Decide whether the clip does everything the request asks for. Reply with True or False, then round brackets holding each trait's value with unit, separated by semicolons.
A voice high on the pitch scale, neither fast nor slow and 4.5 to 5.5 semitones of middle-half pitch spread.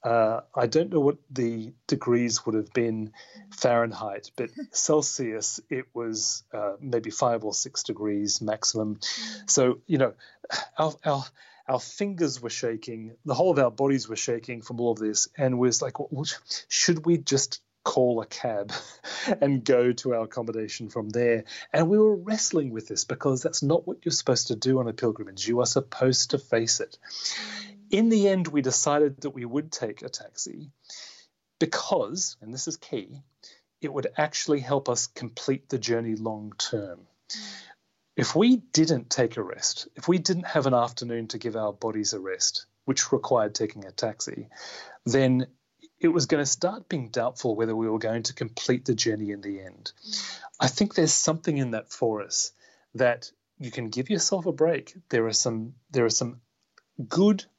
False (130 Hz; 180 wpm; 5.2 semitones)